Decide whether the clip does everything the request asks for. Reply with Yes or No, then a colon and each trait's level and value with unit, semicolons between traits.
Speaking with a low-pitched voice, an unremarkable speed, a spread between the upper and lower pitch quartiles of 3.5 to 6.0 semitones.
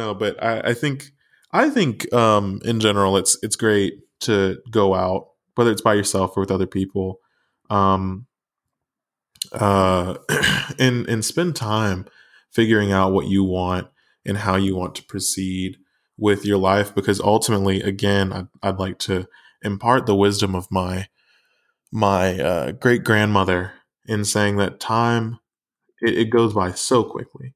No: low, 100 Hz; average, 150 wpm; average, 2.8 semitones